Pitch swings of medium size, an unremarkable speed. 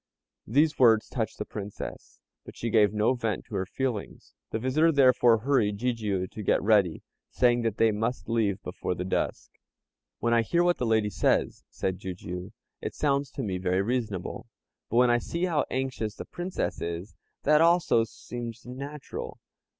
Yes: average, 4.0 semitones; average, 175 wpm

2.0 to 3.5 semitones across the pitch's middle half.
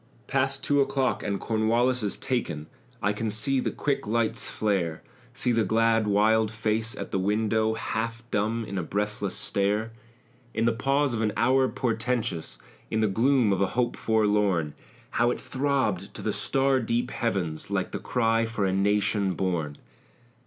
Yes: average, 2.8 semitones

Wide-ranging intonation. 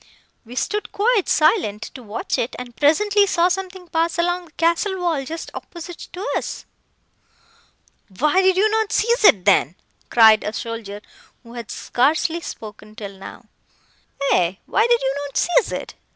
Yes: wide, 8.8 semitones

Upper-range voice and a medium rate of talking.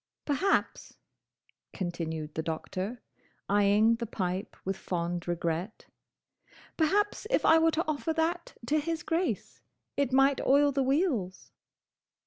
No: high, 240 Hz; slow, 120 wpm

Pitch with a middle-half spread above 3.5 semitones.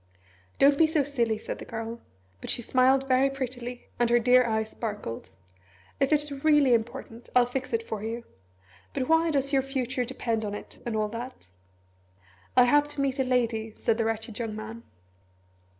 No: average, 3.2 semitones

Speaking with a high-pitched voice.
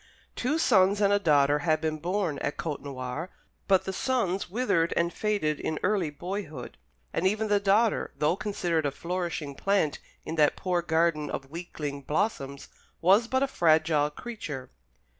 No: medium, 170 Hz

